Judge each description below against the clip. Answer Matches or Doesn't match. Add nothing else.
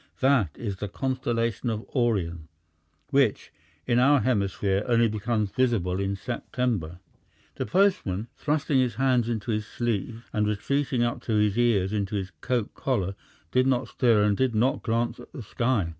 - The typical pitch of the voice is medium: Doesn't match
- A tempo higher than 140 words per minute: Matches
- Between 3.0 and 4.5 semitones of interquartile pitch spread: Matches